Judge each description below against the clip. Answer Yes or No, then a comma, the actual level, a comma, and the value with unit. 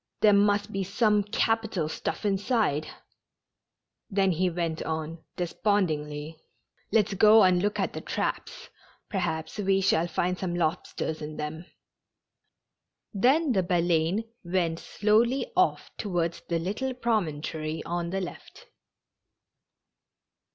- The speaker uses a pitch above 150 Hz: Yes, medium, 185 Hz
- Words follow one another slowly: Yes, slow, 125 wpm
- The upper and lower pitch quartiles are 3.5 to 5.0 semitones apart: Yes, average, 4.2 semitones